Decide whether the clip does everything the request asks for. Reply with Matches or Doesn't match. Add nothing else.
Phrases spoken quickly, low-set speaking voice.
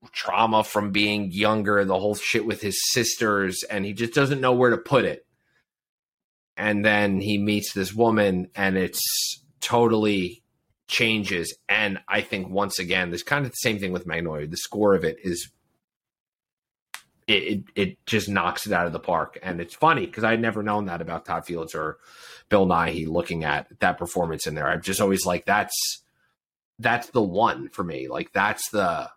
Doesn't match